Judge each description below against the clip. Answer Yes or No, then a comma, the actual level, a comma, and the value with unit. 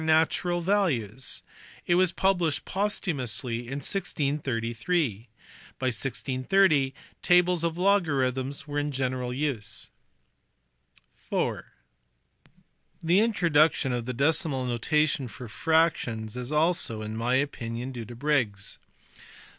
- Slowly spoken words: Yes, slow, 105 wpm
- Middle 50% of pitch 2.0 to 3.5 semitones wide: No, average, 5.3 semitones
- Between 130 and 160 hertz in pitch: Yes, medium, 140 Hz